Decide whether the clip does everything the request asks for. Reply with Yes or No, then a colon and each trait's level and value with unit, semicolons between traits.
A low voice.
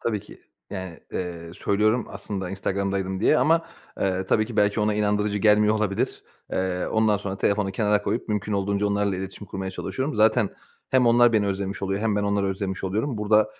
Yes: low, 100 Hz